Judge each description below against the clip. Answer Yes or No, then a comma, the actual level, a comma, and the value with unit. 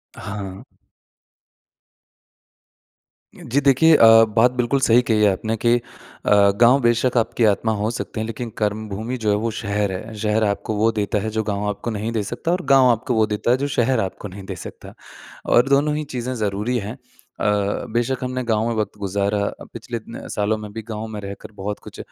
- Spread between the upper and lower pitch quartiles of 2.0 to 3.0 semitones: Yes, narrow, 2.6 semitones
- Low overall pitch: Yes, low, 110 Hz